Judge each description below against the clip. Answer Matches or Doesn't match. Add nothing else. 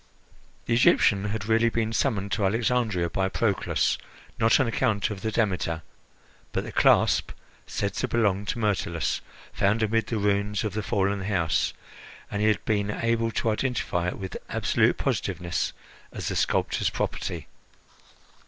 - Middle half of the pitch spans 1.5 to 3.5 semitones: Matches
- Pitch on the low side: Matches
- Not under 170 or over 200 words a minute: Doesn't match